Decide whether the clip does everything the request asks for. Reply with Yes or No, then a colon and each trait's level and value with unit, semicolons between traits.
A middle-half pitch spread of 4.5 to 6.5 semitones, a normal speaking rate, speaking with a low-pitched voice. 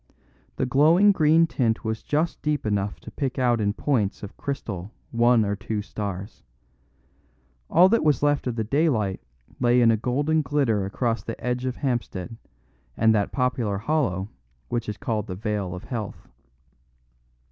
Yes: average, 5.2 semitones; average, 160 wpm; low, 115 Hz